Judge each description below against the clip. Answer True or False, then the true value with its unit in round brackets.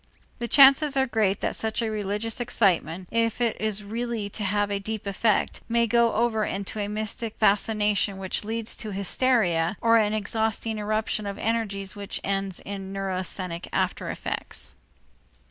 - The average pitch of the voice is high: True (215 Hz)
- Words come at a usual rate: True (165 wpm)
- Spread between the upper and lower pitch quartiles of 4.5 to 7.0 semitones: False (2.5 semitones)